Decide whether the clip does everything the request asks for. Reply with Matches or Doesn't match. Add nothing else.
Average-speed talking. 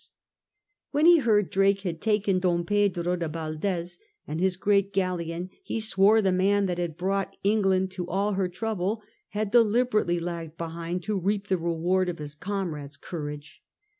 Matches